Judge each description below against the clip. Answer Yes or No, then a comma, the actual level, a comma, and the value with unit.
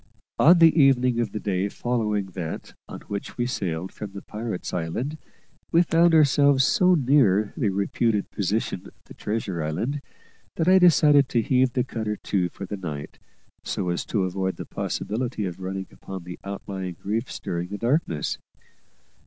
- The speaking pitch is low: Yes, low, 105 Hz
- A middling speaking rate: Yes, average, 170 wpm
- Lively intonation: Yes, wide, 5.8 semitones